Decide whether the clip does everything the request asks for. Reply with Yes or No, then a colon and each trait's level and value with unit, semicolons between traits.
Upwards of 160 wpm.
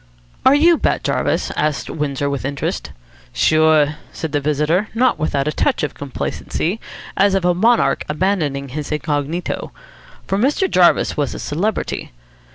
No: average, 150 wpm